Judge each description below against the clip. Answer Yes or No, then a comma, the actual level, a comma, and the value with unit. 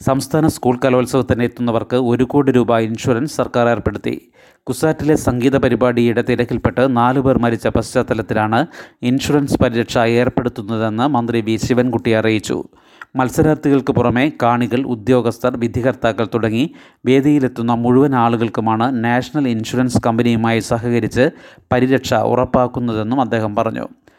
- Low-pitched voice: Yes, low, 120 Hz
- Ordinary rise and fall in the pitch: No, narrow, 1.8 semitones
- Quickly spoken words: No, average, 100 wpm